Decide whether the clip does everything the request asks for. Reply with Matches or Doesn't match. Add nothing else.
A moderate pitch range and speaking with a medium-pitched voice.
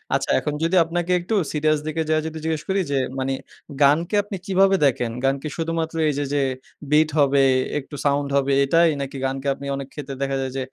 Matches